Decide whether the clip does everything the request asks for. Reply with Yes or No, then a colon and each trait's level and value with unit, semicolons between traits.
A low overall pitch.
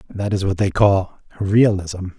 Yes: low, 100 Hz